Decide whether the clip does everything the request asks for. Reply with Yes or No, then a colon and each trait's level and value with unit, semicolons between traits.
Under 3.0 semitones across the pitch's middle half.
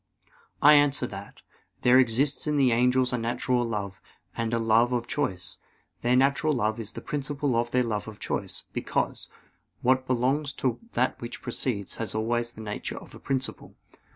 Yes: narrow, 2.5 semitones